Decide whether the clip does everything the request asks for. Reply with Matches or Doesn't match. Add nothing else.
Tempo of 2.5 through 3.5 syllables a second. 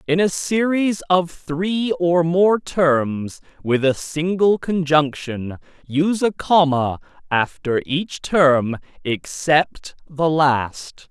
Matches